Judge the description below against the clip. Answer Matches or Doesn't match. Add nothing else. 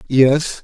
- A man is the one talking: Matches